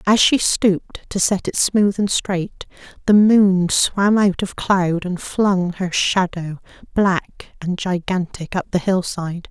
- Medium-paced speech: Yes, average, 160 wpm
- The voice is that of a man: No, female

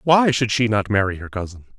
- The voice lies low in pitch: Yes, low, 115 Hz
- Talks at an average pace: No, fast, 235 wpm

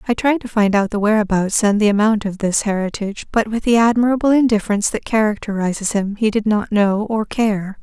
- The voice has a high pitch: Yes, high, 215 Hz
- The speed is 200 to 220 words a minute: Yes, fast, 205 wpm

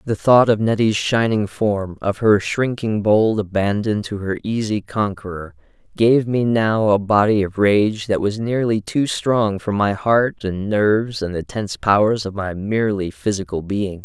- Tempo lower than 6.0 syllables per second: Yes, 4.3 syllables/s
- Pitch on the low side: Yes, low, 105 Hz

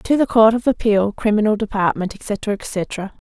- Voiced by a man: No, female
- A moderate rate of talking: Yes, average, 165 wpm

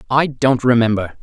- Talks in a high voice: No, low, 125 Hz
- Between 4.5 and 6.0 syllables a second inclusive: Yes, 5.0 syllables/s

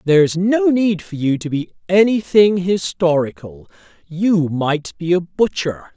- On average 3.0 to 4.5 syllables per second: Yes, 4.0 syllables/s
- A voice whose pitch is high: No, medium, 175 Hz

